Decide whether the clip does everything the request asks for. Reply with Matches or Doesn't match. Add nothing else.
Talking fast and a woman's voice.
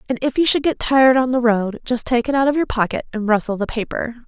Matches